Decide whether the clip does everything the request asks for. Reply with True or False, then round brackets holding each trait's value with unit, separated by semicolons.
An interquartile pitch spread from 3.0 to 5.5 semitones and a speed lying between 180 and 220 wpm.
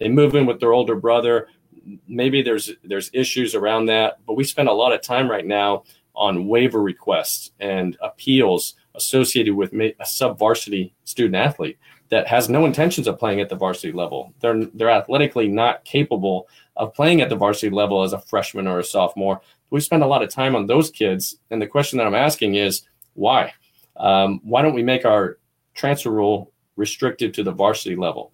True (4.7 semitones; 195 wpm)